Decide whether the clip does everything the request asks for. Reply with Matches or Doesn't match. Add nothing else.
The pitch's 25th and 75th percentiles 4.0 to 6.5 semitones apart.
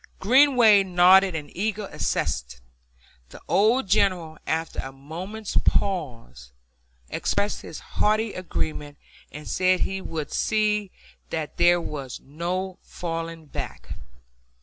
Matches